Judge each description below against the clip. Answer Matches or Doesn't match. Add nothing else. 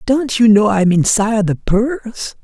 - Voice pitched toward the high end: Matches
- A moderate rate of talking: Matches